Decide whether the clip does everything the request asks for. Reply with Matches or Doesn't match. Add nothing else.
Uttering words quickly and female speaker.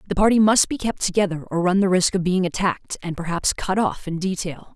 Matches